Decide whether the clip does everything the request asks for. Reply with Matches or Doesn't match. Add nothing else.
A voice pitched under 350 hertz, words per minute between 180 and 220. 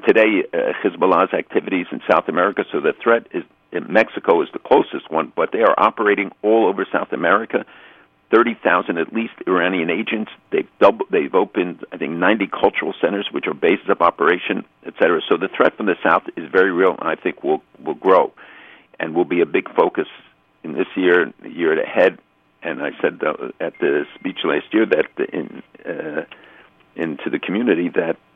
Doesn't match